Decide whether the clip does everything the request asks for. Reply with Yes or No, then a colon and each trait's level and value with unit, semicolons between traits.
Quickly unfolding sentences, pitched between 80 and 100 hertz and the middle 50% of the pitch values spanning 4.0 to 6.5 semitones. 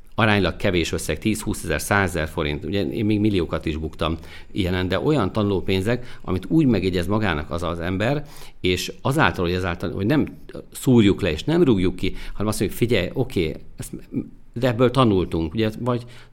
Yes: fast, 175 wpm; very low, 95 Hz; average, 4.4 semitones